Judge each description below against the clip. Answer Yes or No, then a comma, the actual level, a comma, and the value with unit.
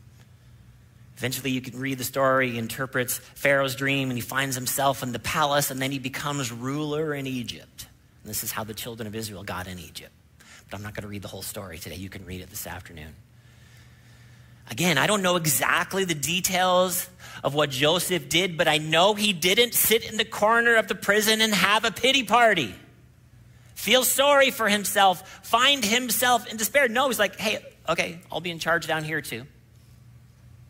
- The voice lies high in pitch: No, low, 135 Hz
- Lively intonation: Yes, wide, 8.2 semitones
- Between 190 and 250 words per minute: Yes, average, 195 wpm